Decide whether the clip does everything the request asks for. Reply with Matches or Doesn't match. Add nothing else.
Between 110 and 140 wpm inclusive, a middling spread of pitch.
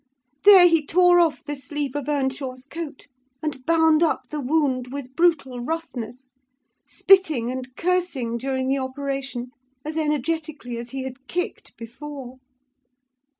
Matches